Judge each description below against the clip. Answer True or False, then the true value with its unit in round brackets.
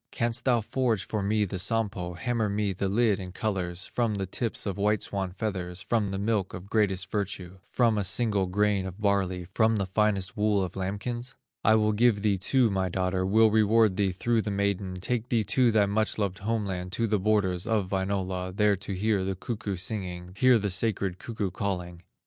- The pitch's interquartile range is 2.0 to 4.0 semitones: True (2.6 semitones)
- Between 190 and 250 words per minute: True (200 wpm)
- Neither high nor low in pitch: False (100 Hz)